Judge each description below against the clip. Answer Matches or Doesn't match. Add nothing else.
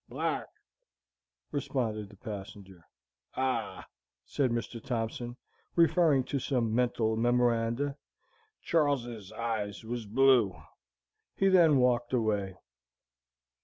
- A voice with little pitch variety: Doesn't match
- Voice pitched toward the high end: Doesn't match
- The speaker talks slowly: Matches